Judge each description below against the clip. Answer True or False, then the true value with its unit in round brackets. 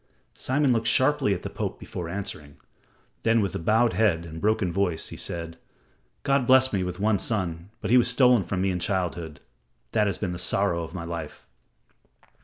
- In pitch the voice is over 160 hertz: False (100 Hz)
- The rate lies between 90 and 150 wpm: False (190 wpm)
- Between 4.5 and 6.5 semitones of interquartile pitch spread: True (4.9 semitones)